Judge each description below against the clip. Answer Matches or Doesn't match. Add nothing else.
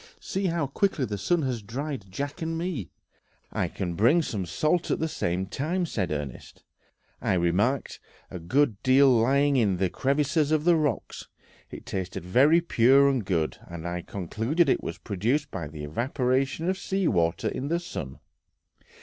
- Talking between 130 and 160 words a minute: Doesn't match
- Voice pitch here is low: Matches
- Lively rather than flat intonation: Matches